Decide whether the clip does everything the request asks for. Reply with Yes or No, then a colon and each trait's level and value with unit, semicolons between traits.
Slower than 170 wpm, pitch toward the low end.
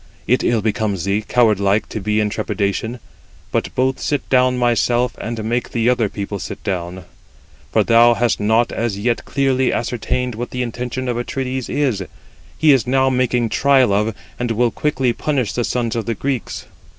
No: average, 180 wpm; low, 120 Hz